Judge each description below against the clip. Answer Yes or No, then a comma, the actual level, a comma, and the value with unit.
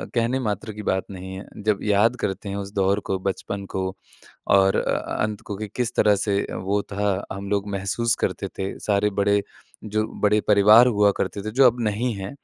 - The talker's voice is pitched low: Yes, low, 100 Hz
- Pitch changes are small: Yes, narrow, 1.6 semitones